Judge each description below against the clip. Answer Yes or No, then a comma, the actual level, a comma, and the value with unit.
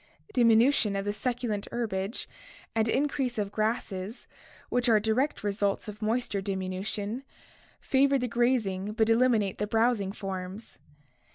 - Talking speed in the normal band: No, slow, 125 wpm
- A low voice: No, high, 220 Hz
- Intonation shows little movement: No, average, 3.3 semitones